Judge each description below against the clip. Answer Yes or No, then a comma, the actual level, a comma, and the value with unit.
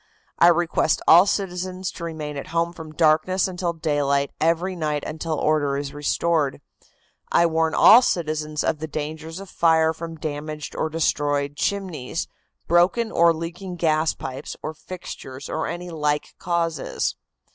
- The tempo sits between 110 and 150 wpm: Yes, average, 145 wpm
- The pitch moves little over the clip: Yes, narrow, 2.3 semitones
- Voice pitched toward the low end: No, medium, 160 Hz